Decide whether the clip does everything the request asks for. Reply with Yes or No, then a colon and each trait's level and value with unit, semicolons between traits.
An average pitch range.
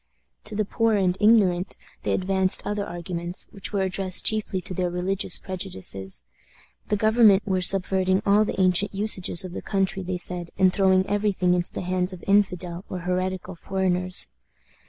No: narrow, 1.7 semitones